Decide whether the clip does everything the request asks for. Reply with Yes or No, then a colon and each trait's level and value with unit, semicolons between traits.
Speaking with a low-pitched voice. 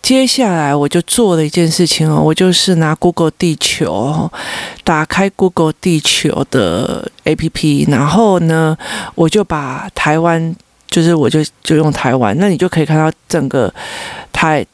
No: medium, 165 Hz